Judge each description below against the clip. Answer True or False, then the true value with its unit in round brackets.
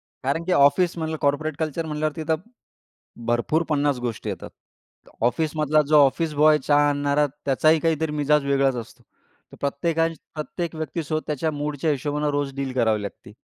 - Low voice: False (150 Hz)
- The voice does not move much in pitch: True (2.1 semitones)